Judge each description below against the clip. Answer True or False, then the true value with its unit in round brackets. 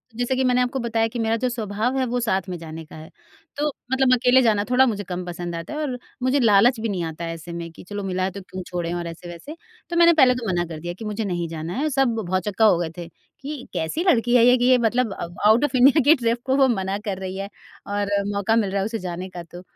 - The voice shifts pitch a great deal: True (5.9 semitones)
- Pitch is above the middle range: True (215 Hz)